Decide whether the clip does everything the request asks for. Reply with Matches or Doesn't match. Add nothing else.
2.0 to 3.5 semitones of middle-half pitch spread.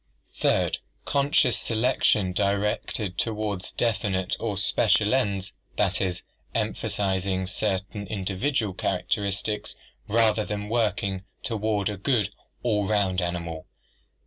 Matches